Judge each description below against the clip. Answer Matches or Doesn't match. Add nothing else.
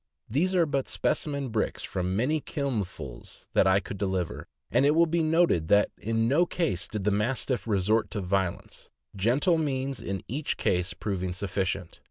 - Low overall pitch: Matches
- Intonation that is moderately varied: Doesn't match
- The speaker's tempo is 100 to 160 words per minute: Doesn't match